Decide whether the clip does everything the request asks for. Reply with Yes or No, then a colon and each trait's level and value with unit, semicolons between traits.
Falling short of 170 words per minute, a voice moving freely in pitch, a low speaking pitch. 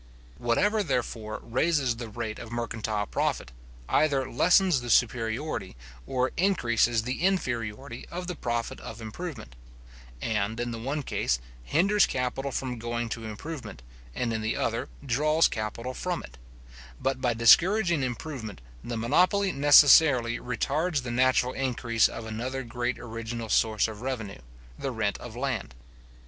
No: average, 140 wpm; average, 4.1 semitones; low, 120 Hz